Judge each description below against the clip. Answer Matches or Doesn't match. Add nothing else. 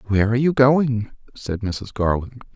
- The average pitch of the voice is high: Doesn't match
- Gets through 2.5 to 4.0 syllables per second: Doesn't match